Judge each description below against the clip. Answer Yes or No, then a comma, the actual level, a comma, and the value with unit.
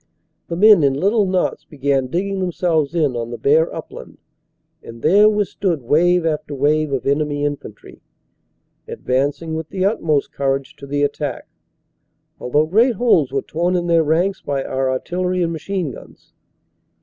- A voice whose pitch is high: No, medium, 155 Hz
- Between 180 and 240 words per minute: No, average, 155 wpm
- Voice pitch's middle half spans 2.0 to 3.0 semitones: No, average, 4.5 semitones